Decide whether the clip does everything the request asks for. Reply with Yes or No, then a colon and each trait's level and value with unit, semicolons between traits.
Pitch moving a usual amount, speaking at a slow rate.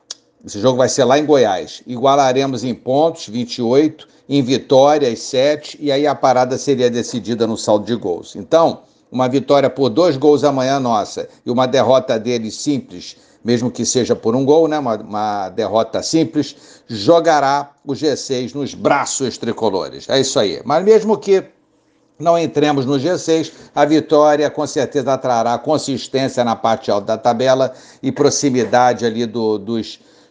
No: average, 3.4 semitones; average, 160 wpm